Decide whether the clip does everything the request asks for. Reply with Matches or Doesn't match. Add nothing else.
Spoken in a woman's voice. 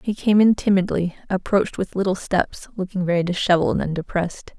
Matches